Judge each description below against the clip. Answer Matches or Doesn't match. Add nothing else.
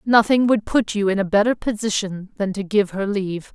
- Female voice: Matches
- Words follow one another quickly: Matches